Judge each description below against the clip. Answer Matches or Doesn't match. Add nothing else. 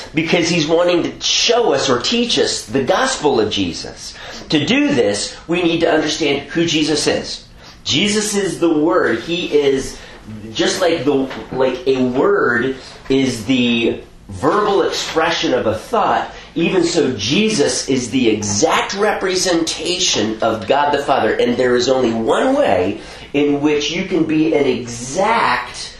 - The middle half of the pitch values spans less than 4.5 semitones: Doesn't match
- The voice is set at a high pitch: Doesn't match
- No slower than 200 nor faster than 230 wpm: Doesn't match